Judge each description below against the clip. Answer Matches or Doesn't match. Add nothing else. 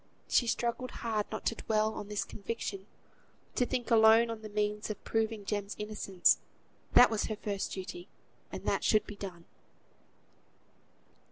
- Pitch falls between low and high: Doesn't match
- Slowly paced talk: Doesn't match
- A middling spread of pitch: Doesn't match